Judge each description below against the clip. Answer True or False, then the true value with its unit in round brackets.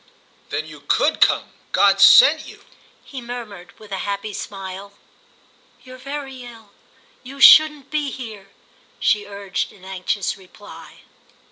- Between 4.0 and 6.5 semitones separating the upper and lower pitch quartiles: True (5.0 semitones)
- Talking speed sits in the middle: False (125 wpm)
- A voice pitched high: True (210 Hz)